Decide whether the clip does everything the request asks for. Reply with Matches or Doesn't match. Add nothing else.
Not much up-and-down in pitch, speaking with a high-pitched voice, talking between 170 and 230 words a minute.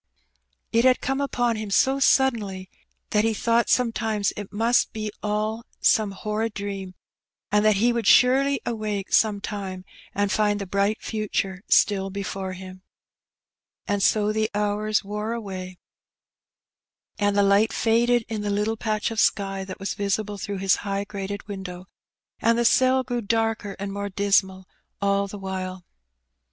Doesn't match